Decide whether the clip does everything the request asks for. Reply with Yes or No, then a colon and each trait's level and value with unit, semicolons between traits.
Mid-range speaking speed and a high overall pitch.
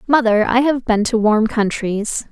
Yes: average, 180 wpm; high, 230 Hz